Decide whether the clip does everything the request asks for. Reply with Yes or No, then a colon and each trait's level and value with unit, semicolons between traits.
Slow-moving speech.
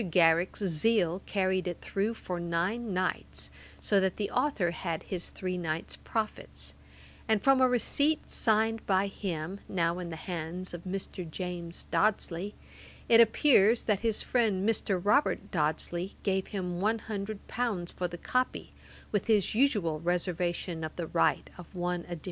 No: average, 155 wpm